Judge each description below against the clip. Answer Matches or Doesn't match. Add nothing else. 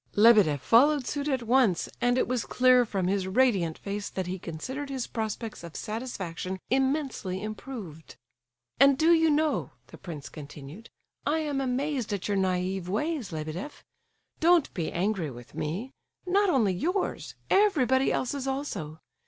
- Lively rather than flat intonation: Matches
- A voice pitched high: Matches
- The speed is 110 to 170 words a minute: Matches